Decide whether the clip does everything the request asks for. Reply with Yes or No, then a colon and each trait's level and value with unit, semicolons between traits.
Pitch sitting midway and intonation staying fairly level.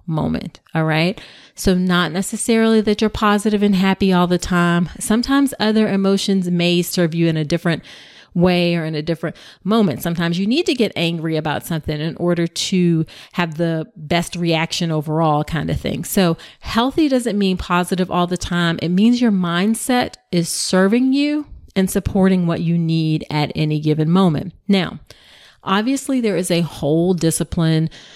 No: medium, 175 Hz; average, 3.5 semitones